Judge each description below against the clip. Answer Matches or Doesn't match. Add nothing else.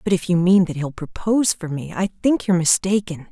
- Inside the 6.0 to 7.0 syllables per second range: Doesn't match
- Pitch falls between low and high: Matches